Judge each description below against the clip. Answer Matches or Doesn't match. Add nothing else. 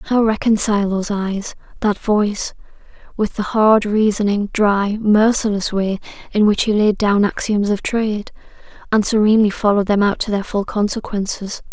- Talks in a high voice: Matches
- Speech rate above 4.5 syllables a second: Matches